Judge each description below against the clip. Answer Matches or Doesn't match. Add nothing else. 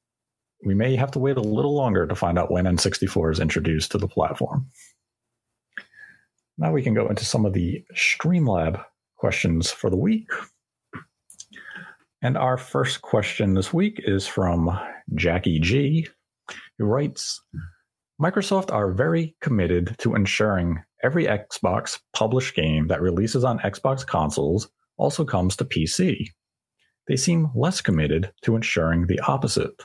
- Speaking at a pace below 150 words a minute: Matches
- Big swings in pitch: Matches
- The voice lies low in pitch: Matches